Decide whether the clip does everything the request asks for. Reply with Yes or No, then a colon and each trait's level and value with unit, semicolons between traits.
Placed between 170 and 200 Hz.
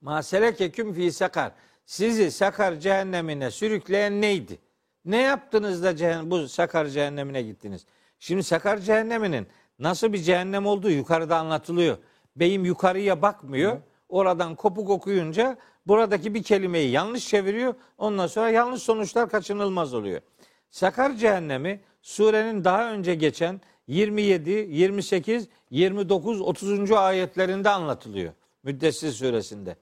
Yes: high, 190 Hz